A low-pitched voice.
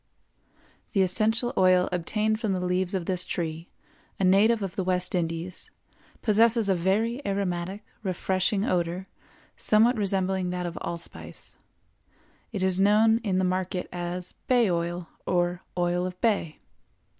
No: medium, 185 Hz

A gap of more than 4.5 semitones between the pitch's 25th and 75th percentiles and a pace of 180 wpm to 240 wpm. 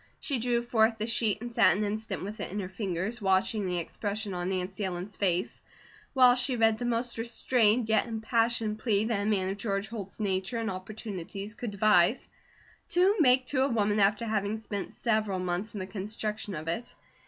No: average, 2.9 semitones; average, 195 wpm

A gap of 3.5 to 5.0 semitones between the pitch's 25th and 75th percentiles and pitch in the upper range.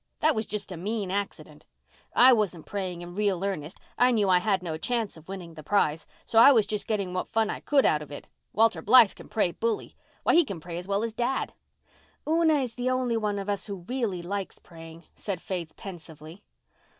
Yes: average, 4.5 semitones; high, 200 Hz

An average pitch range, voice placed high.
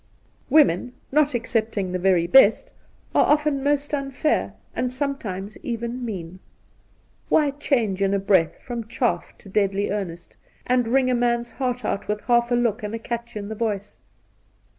Yes: average, 4.1 semitones; high, 235 Hz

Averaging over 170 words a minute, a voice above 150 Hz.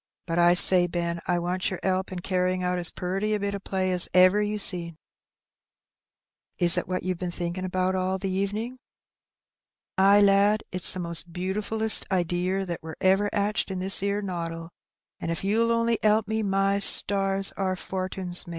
Yes: average, 185 wpm; medium, 185 Hz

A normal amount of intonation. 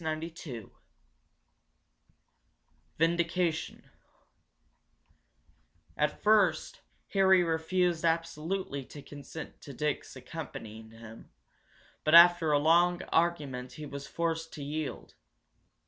Yes: average, 3.2 semitones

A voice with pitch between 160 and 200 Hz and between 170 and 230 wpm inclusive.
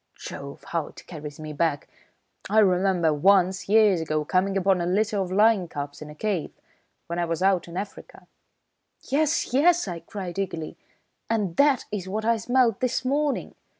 Yes: high, 190 Hz; average, 180 wpm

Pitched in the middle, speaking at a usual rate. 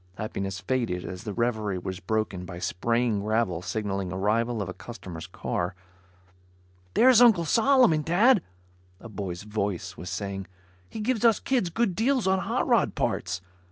No: low, 110 Hz; average, 155 wpm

